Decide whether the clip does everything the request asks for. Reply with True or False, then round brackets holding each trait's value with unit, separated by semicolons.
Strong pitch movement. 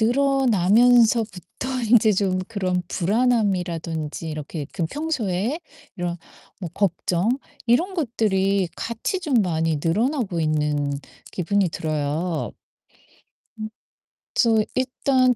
True (6.0 semitones)